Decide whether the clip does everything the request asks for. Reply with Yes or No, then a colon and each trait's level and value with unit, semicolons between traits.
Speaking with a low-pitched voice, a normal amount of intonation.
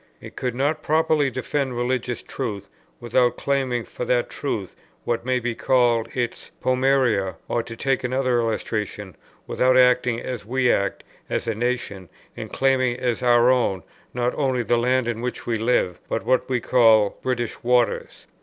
No: low, 125 Hz; narrow, 1.8 semitones